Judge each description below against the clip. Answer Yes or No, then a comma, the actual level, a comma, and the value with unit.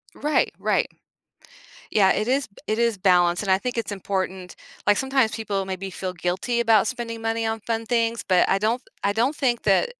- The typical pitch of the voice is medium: No, high, 220 Hz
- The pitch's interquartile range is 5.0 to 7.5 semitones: No, average, 3.5 semitones